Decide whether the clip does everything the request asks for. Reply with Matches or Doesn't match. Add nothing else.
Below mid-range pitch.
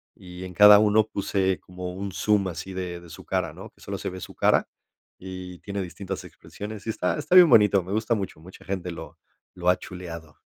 Matches